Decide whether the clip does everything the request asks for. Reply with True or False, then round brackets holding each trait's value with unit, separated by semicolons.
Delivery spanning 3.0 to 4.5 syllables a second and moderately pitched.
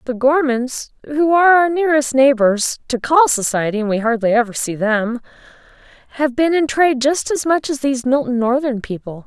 False (4.0 syllables/s; 265 Hz)